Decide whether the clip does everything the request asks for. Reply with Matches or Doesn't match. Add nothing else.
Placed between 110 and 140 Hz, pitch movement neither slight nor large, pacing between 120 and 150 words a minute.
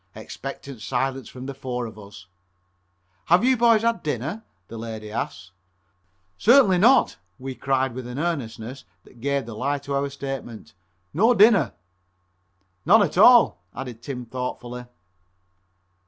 Doesn't match